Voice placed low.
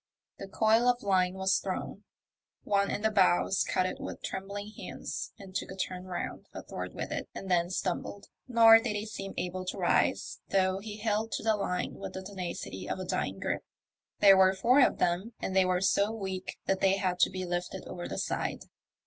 No: high, 190 Hz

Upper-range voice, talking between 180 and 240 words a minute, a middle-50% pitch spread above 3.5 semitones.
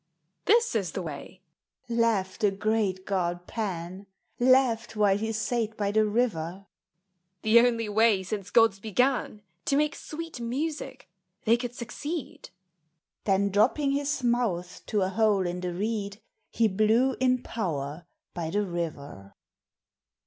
No: high, 215 Hz; average, 140 wpm; average, 4.2 semitones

